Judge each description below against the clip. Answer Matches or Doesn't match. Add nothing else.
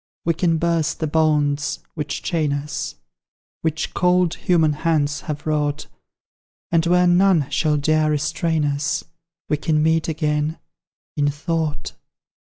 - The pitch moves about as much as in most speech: Doesn't match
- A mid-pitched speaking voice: Matches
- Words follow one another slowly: Matches